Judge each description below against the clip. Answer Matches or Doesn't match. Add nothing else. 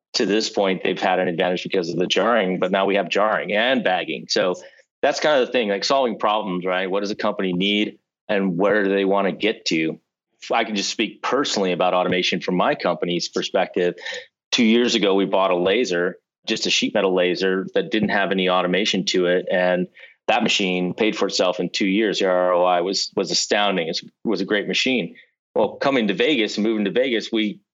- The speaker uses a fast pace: Matches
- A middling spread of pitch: Doesn't match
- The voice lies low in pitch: Matches